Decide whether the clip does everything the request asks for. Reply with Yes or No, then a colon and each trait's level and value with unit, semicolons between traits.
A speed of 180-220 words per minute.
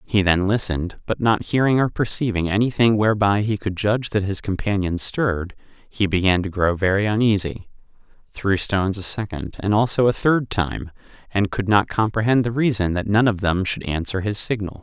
Yes: average, 185 wpm